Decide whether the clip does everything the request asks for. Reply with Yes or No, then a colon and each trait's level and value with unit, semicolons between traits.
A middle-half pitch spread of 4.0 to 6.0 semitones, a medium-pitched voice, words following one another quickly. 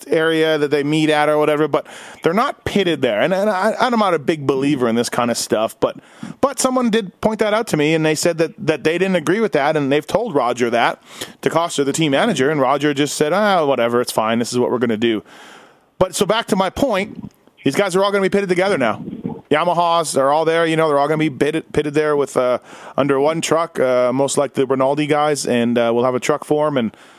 Yes: average, 5.1 semitones; medium, 155 Hz; fast, 265 wpm